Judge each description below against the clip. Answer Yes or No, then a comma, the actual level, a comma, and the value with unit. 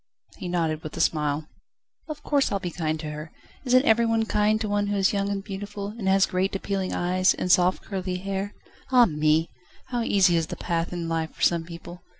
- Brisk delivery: Yes, fast, 215 wpm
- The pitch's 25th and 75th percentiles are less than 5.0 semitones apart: Yes, average, 3.5 semitones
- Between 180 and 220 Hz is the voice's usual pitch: Yes, medium, 185 Hz